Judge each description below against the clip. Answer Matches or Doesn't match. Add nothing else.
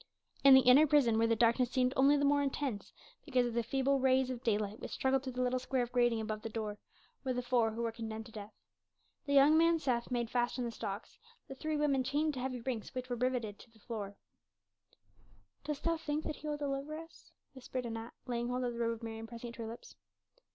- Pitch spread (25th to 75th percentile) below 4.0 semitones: Matches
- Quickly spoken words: Matches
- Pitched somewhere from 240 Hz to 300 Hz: Matches